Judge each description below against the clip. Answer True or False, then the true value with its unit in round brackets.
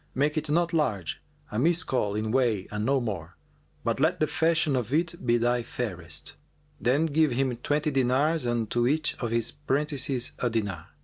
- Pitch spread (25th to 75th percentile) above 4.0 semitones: True (4.6 semitones)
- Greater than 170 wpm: True (180 wpm)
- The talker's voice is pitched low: True (130 Hz)